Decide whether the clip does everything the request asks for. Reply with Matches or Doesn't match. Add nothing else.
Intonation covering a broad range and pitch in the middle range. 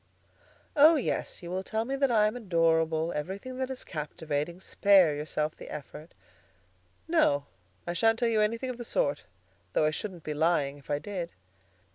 Matches